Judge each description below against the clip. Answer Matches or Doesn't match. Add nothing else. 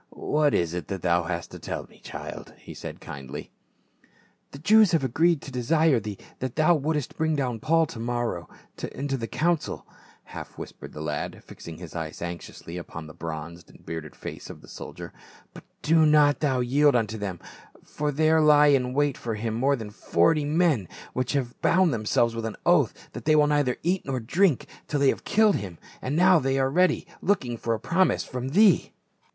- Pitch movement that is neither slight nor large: Doesn't match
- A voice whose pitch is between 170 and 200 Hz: Doesn't match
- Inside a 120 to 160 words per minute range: Doesn't match